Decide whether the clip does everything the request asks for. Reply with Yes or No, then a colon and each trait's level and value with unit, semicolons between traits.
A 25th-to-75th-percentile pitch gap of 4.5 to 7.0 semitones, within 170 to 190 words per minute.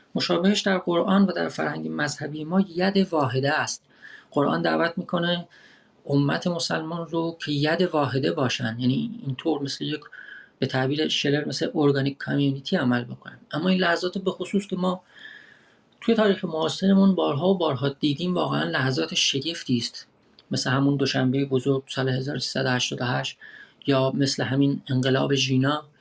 No: average, 4.8 semitones; average, 145 wpm